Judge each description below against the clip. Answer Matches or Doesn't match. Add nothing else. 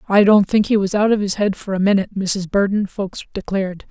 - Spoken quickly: Matches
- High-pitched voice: Matches